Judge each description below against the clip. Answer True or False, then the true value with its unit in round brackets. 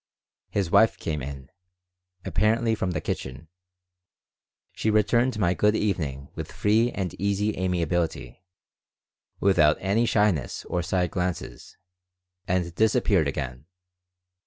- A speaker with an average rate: False (110 wpm)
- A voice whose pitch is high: False (95 Hz)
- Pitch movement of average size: True (4.6 semitones)